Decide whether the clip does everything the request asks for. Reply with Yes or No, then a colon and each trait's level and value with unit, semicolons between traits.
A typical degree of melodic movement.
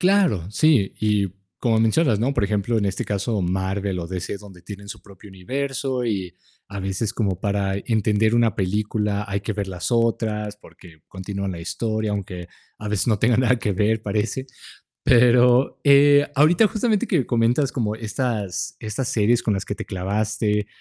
Yes: average, 3.4 semitones